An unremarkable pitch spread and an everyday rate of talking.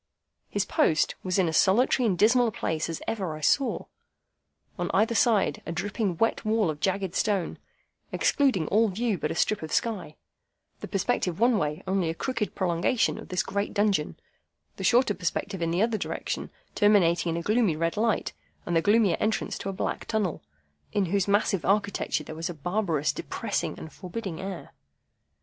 Yes: average, 4.3 semitones; average, 180 wpm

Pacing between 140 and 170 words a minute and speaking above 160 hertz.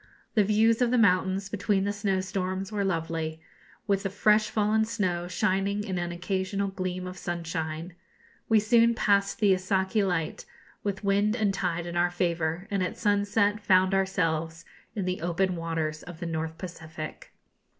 Yes: average, 160 wpm; high, 190 Hz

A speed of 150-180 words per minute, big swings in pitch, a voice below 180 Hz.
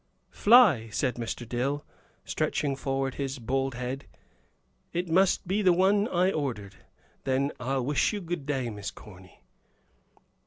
No: average, 140 wpm; wide, 6.0 semitones; low, 135 Hz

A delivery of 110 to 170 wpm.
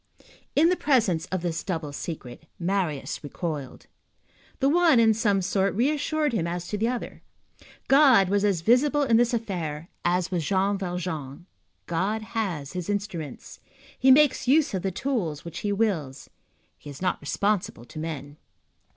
Yes: average, 160 wpm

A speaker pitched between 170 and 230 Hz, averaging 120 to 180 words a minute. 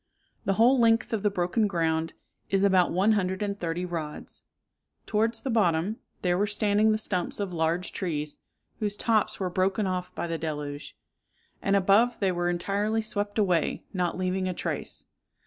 Yes: high, 190 Hz; average, 170 wpm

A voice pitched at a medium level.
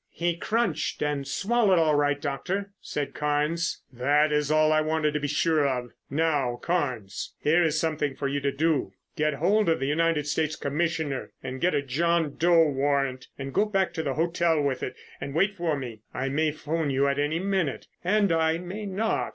Yes: medium, 155 Hz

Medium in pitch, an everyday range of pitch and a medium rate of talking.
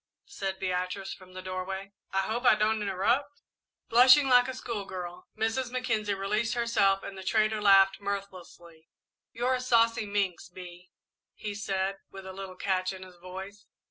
No: high, 195 Hz; average, 3.1 semitones; average, 160 wpm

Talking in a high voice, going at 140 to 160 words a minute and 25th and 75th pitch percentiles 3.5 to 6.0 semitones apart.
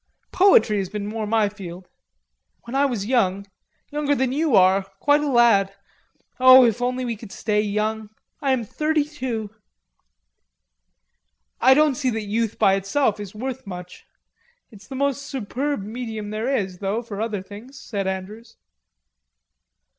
Yes: high, 225 Hz; average, 150 wpm; average, 4.5 semitones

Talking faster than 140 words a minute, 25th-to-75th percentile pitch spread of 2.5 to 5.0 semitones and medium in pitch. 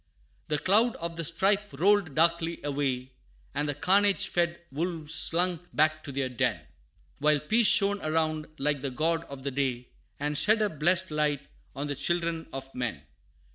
Yes: average, 170 wpm; average, 3.5 semitones; medium, 155 Hz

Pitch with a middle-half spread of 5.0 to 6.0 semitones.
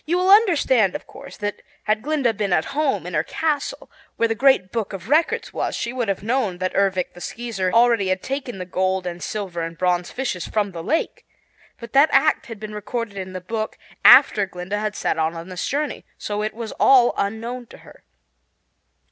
Yes: wide, 5.5 semitones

